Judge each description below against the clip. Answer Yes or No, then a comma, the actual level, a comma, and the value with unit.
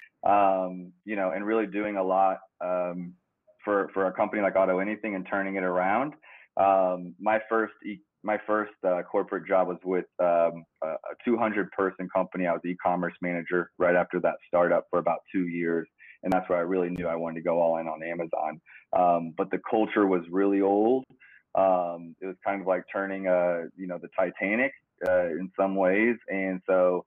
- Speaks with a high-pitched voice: No, very low, 95 Hz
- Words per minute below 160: No, average, 195 wpm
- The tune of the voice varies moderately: No, narrow, 1.8 semitones